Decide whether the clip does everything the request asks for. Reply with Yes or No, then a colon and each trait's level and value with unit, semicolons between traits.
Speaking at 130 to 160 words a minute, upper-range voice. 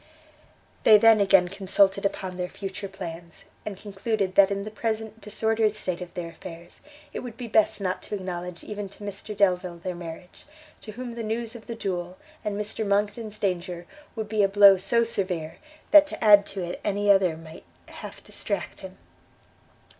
No: average, 180 wpm; high, 200 Hz